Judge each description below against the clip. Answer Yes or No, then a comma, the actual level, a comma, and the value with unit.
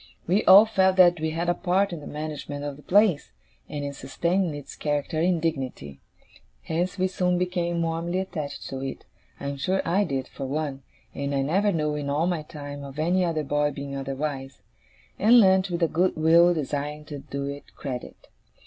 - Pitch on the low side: No, medium, 155 Hz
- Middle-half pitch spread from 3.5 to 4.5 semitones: Yes, average, 4.0 semitones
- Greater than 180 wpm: Yes, average, 195 wpm